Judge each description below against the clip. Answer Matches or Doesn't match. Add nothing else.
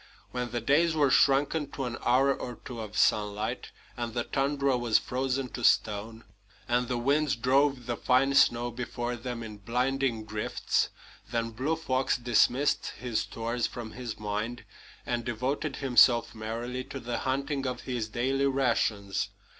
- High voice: Doesn't match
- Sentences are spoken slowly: Doesn't match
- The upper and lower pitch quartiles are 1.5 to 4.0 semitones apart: Matches